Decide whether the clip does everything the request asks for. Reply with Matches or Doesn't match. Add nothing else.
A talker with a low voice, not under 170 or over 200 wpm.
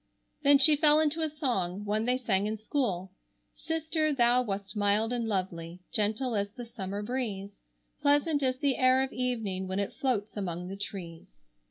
Doesn't match